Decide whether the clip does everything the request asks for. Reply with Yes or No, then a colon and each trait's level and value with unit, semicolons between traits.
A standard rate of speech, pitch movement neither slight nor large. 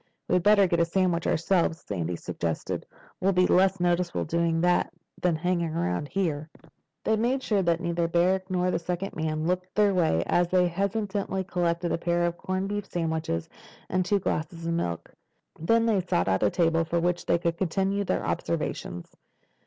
No: average, 180 wpm; narrow, 2.2 semitones